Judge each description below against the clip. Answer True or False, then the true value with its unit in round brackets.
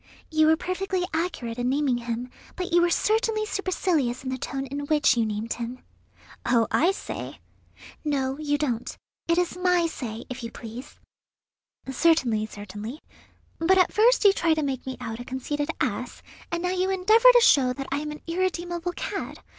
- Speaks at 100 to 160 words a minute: False (180 wpm)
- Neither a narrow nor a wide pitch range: False (6.2 semitones)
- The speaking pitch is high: True (300 Hz)